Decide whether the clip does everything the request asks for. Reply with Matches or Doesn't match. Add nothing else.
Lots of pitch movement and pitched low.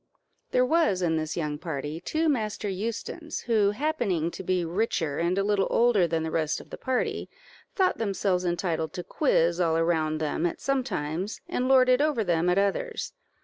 Doesn't match